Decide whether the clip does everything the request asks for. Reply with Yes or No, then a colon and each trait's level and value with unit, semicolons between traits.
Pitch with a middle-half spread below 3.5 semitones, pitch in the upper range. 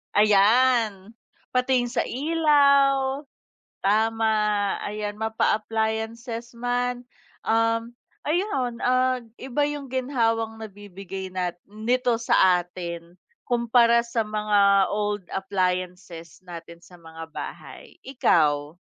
No: average, 4.3 semitones; high, 220 Hz